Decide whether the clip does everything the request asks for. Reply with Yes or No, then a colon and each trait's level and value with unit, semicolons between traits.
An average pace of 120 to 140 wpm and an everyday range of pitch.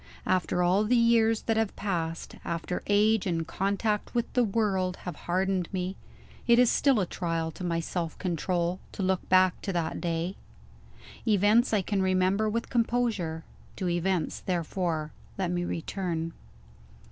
No: average, 155 wpm; average, 3.4 semitones